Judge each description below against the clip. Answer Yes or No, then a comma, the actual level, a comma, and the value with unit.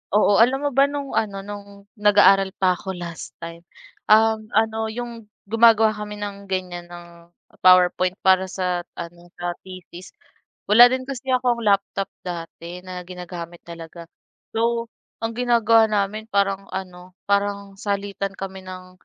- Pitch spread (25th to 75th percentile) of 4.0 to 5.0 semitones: No, average, 3.3 semitones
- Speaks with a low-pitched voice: No, high, 200 Hz